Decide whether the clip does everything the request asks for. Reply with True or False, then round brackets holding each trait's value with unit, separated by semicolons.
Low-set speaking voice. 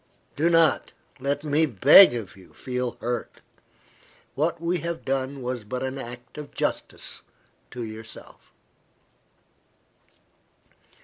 True (130 Hz)